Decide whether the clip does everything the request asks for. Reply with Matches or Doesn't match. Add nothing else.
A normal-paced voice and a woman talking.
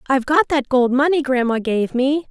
Doesn't match